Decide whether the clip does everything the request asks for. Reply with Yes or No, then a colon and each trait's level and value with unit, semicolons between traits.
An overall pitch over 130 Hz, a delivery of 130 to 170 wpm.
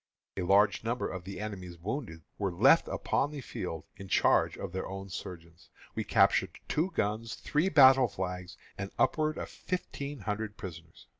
No: low, 100 Hz; average, 165 wpm